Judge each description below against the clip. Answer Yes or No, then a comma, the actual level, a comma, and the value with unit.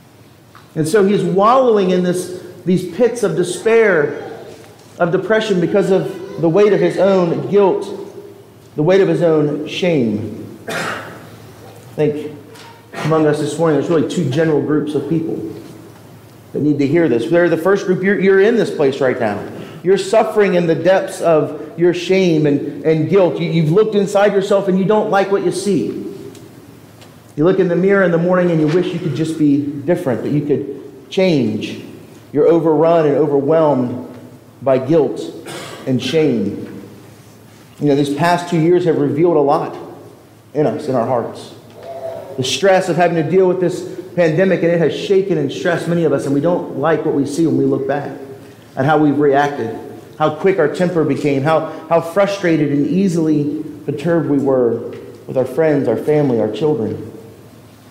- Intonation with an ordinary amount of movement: Yes, average, 4.6 semitones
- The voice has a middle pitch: Yes, medium, 160 Hz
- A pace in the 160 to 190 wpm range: Yes, average, 180 wpm